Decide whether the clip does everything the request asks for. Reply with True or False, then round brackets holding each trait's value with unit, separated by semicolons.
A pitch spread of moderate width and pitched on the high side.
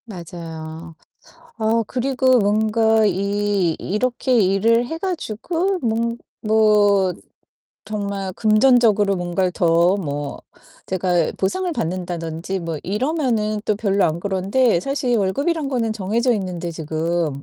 True (4.8 semitones; 205 Hz)